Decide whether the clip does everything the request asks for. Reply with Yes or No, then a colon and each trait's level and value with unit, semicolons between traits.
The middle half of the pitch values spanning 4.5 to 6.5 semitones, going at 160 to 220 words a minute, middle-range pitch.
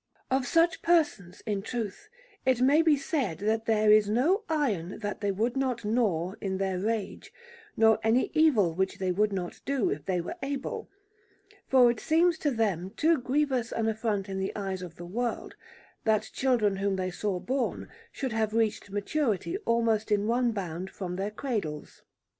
No: average, 4.8 semitones; average, 175 wpm; high, 220 Hz